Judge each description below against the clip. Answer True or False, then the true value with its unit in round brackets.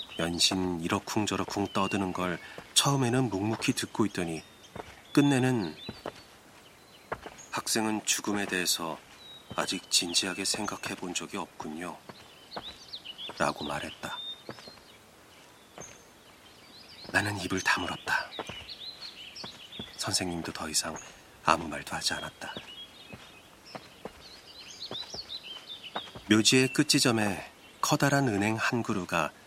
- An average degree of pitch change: True (4.6 semitones)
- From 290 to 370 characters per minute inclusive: False (195 characters per minute)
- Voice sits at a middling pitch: False (100 Hz)